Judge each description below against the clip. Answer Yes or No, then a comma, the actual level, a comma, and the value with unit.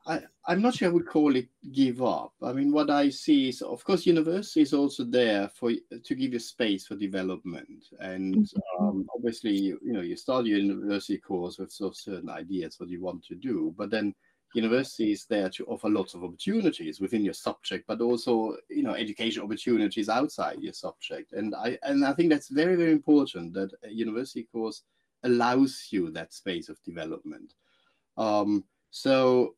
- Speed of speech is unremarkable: Yes, average, 190 wpm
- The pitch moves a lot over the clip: Yes, wide, 8.1 semitones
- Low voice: Yes, low, 125 Hz